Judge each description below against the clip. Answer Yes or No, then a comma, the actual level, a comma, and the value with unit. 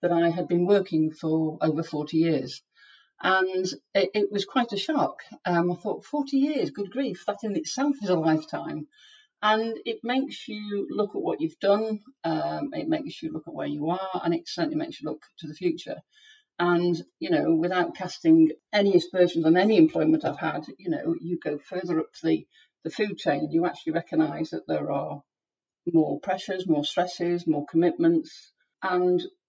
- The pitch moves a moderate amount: No, wide, 6.7 semitones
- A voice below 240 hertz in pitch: Yes, medium, 185 Hz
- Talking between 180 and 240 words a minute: Yes, average, 185 wpm